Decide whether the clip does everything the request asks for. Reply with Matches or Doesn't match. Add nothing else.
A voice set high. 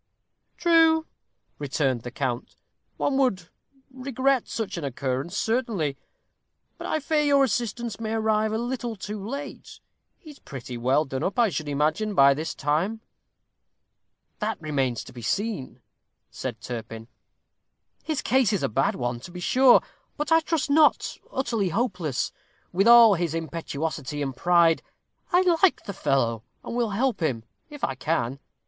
Matches